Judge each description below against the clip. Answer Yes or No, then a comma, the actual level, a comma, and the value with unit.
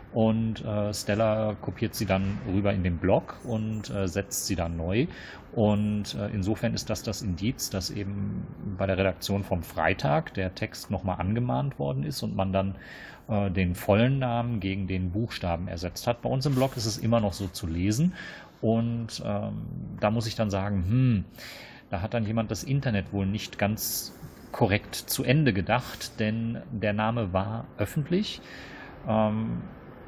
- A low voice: Yes, low, 105 Hz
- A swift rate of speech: No, average, 170 wpm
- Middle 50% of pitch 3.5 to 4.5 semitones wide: No, average, 3.0 semitones